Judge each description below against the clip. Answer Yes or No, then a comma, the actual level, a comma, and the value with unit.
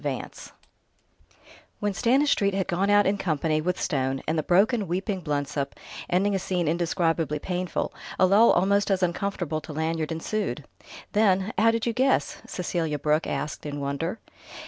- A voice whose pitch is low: No, medium, 180 Hz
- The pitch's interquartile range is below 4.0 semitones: No, average, 4.3 semitones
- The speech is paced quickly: No, average, 160 wpm